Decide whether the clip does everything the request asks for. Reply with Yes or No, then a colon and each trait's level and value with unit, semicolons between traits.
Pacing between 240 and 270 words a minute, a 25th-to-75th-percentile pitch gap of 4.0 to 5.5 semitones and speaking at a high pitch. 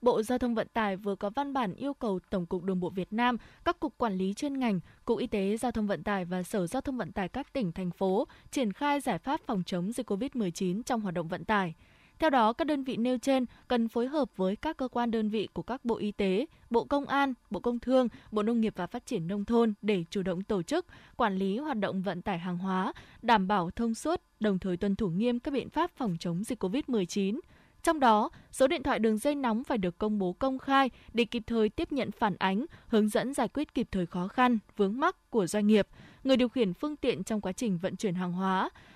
Yes: fast, 250 wpm; average, 4.7 semitones; high, 225 Hz